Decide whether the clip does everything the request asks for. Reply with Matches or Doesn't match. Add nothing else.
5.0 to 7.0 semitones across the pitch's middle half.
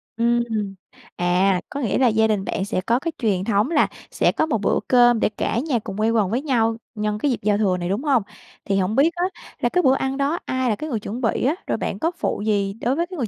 Doesn't match